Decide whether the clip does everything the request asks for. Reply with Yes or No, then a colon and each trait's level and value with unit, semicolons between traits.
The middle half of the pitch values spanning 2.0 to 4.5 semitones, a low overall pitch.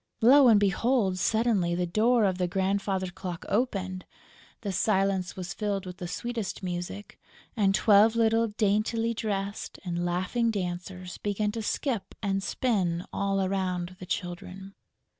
No: average, 3.0 semitones; high, 195 Hz